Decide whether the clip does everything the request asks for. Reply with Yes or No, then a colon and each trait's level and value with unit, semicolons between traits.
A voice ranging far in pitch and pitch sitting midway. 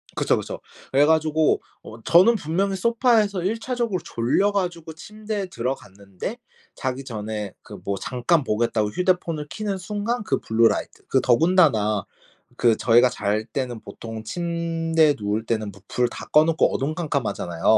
Yes: wide, 8.4 semitones; medium, 150 Hz